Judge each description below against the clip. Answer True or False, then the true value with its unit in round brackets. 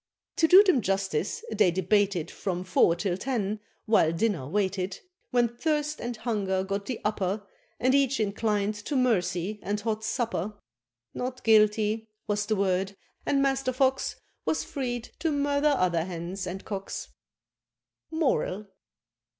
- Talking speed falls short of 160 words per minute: True (140 wpm)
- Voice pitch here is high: True (210 Hz)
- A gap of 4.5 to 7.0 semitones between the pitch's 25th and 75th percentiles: True (4.8 semitones)